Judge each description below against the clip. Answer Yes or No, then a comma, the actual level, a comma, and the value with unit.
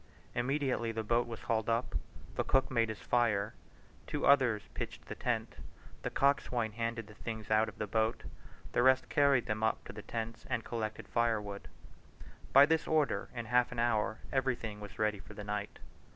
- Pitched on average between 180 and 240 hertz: No, low, 115 Hz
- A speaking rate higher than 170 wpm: Yes, average, 180 wpm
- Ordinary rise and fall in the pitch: No, narrow, 2.3 semitones